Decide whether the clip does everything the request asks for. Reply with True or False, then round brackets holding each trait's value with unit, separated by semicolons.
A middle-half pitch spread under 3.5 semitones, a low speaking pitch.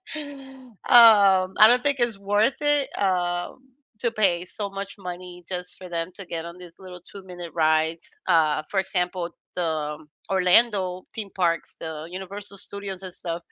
False (2.8 semitones; 185 Hz)